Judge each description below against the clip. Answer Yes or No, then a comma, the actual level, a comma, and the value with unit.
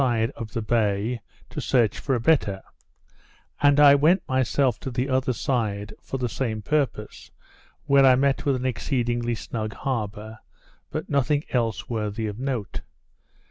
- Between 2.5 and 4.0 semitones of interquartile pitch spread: Yes, average, 3.6 semitones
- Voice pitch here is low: Yes, low, 120 Hz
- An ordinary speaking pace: Yes, average, 155 wpm